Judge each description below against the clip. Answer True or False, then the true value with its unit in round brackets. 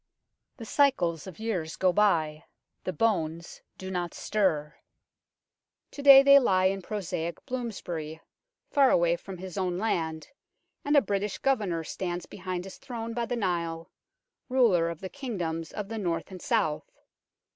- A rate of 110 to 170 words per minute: True (155 wpm)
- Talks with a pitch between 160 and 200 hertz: True (190 Hz)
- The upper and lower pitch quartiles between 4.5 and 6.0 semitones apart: True (5.1 semitones)